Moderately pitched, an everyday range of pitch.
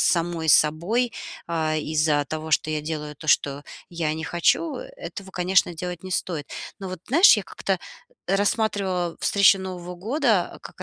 Yes: medium, 175 Hz; average, 3.6 semitones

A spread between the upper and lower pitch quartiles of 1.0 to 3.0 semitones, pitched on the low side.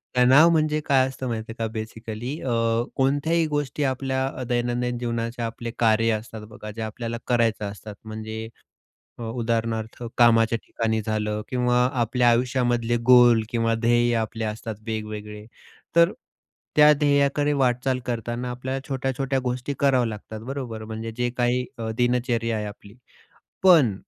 Yes: narrow, 2.6 semitones; low, 120 Hz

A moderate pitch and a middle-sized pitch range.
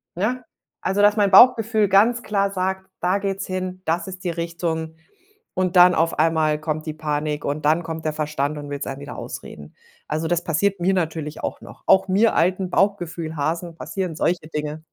Yes: medium, 170 Hz; average, 3.6 semitones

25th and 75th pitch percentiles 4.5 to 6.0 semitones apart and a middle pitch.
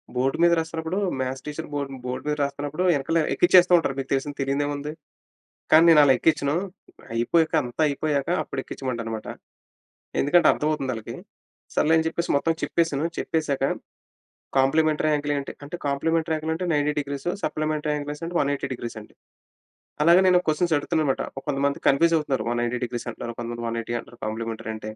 No: average, 3.2 semitones; medium, 145 Hz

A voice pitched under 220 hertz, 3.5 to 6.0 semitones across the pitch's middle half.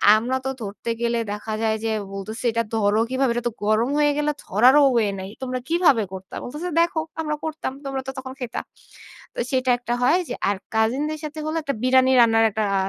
No: high, 245 Hz; average, 4.0 semitones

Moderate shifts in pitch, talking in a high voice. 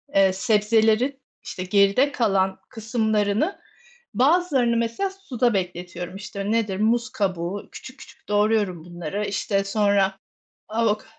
Yes: average, 3.2 semitones; high, 210 Hz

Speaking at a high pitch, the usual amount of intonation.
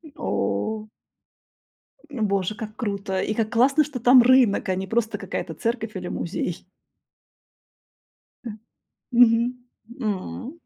Yes: high, 220 Hz; average, 3.7 semitones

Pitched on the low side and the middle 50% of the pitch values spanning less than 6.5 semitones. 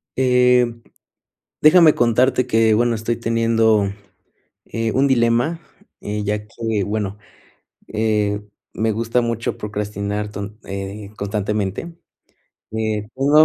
Yes: low, 110 Hz; narrow, 2.4 semitones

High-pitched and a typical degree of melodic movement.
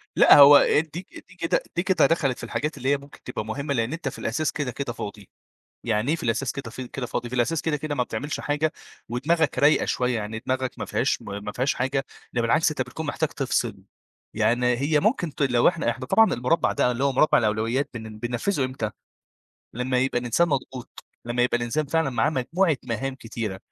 No: low, 130 Hz; average, 3.9 semitones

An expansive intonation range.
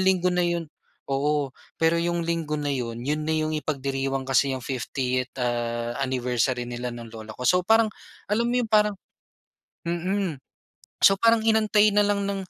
Yes: wide, 7.1 semitones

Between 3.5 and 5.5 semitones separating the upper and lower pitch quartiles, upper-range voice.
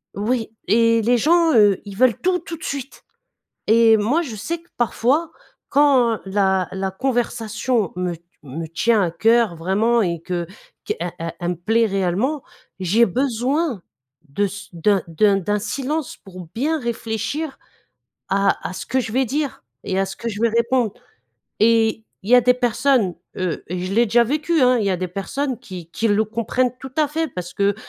Yes: average, 4.9 semitones; high, 225 Hz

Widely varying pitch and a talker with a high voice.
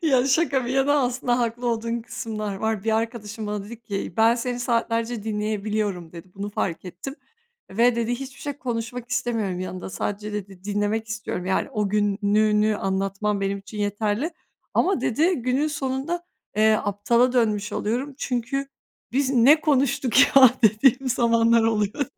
No: average, 3.2 semitones; high, 225 Hz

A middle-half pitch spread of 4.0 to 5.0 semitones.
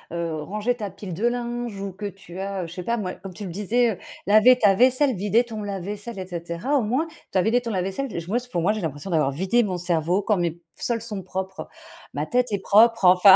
Yes: average, 4.3 semitones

